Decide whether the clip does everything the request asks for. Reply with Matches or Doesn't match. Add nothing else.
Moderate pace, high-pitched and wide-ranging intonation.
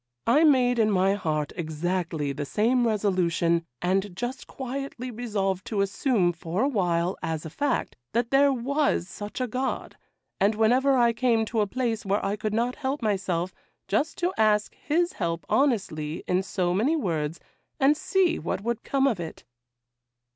Matches